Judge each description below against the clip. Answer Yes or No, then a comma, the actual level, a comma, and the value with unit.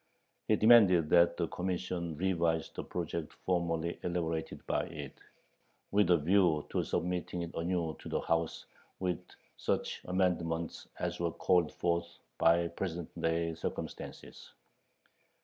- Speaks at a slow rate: Yes, slow, 130 wpm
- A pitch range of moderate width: No, narrow, 1.5 semitones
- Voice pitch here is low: Yes, very low, 85 Hz